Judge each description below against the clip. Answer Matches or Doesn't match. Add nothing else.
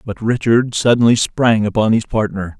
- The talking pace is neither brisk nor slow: Matches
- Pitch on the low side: Matches